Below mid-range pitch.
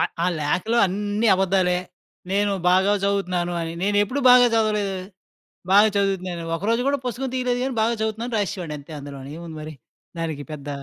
No: high, 195 Hz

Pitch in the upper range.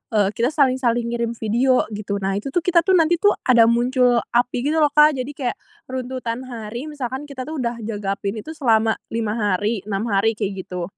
Yes: high, 235 Hz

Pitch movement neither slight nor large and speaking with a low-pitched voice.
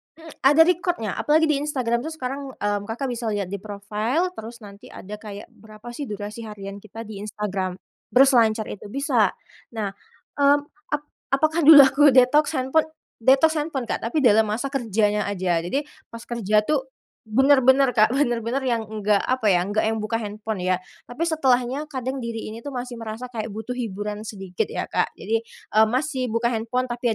No: average, 4.2 semitones; high, 230 Hz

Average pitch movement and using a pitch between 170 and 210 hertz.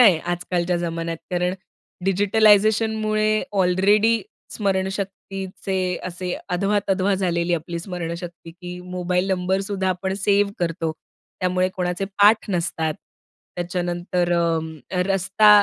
No: narrow, 2.2 semitones; medium, 185 Hz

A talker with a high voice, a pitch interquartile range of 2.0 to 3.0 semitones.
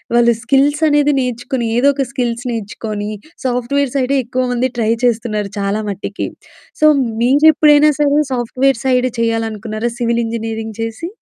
No: high, 240 Hz; average, 3.4 semitones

